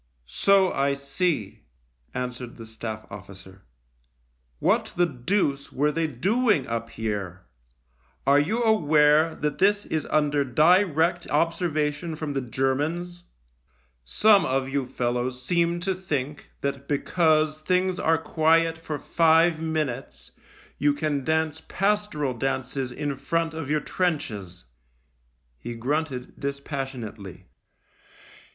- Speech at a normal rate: No, slow, 120 wpm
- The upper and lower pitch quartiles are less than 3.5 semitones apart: No, average, 4.6 semitones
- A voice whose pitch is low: No, medium, 145 Hz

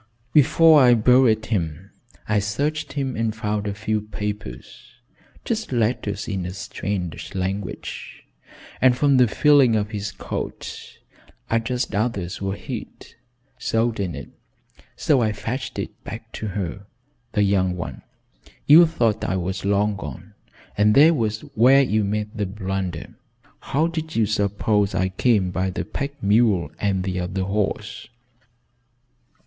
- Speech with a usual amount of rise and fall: Yes, average, 3.9 semitones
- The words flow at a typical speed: Yes, average, 145 wpm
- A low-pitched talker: Yes, low, 105 Hz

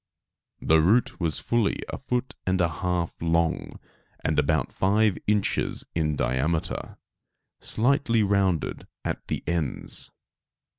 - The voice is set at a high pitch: No, very low, 90 Hz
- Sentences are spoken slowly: Yes, slow, 115 wpm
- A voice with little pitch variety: No, average, 4.7 semitones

